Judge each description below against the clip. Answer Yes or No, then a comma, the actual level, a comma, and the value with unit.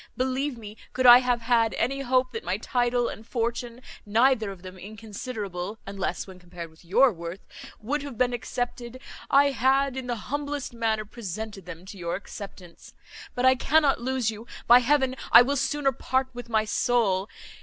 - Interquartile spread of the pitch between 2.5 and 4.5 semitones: Yes, average, 4.0 semitones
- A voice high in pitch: Yes, high, 240 Hz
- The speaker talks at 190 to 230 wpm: No, average, 175 wpm